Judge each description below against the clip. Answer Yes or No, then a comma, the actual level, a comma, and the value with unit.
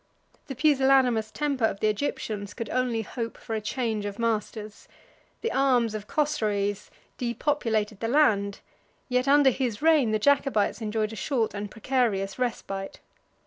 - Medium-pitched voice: No, high, 230 Hz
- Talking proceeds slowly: No, average, 145 wpm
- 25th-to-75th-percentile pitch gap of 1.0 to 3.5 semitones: No, average, 3.9 semitones